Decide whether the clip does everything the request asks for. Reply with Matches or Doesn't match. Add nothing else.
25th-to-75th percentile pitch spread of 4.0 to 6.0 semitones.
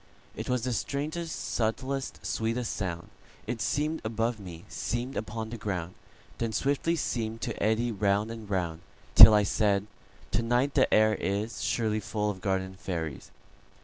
Doesn't match